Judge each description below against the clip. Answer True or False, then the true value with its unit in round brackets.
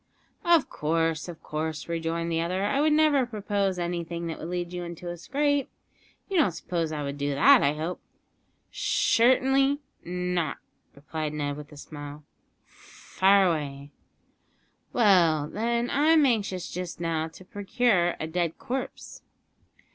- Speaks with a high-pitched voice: False (175 Hz)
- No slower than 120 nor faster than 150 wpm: True (145 wpm)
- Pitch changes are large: True (6.6 semitones)